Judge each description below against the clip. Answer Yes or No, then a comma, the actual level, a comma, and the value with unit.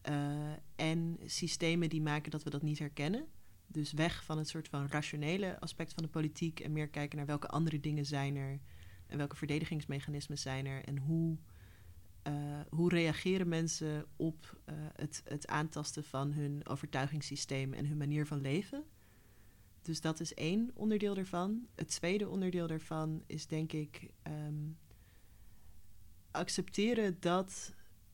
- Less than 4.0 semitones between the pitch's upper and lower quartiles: Yes, average, 2.7 semitones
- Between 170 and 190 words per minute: No, average, 150 wpm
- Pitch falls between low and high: Yes, medium, 150 Hz